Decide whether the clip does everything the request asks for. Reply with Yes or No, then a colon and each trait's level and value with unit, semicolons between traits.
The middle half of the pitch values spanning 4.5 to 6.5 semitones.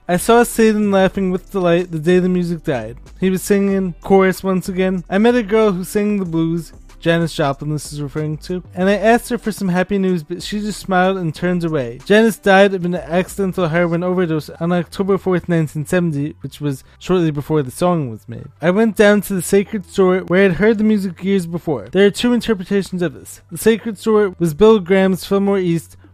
No: average, 3.1 semitones